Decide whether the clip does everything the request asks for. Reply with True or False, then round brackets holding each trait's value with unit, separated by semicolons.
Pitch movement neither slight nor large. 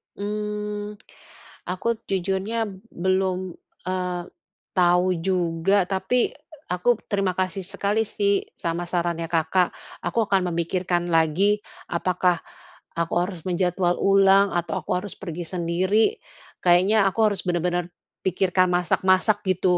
False (2.1 semitones)